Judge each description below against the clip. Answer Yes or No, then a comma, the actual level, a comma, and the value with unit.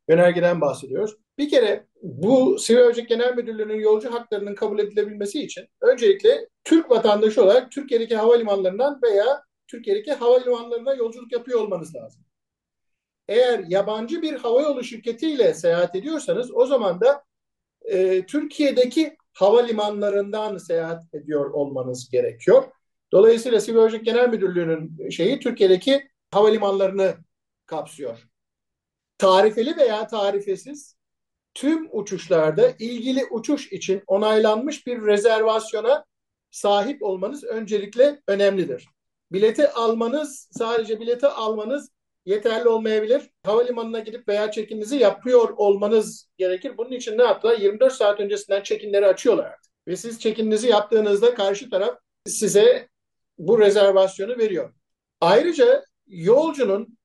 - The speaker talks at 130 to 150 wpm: No, average, 110 wpm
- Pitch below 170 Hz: No, high, 230 Hz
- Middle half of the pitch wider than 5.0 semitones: Yes, wide, 5.6 semitones